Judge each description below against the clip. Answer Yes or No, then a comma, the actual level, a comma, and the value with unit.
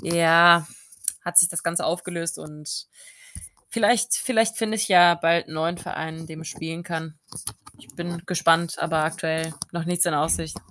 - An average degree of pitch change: No, narrow, 1.4 semitones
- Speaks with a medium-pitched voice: Yes, medium, 170 Hz